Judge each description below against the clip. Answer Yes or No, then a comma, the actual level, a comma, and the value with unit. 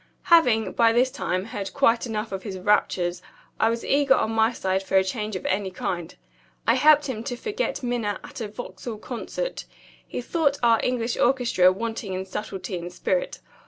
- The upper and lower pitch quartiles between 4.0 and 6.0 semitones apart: Yes, average, 4.5 semitones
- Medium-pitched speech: No, high, 225 Hz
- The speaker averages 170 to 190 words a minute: Yes, average, 185 wpm